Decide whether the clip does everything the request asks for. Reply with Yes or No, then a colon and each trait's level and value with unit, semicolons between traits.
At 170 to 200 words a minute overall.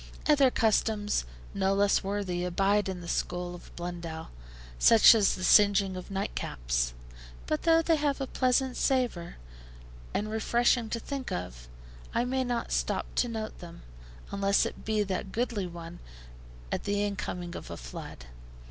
No: average, 155 wpm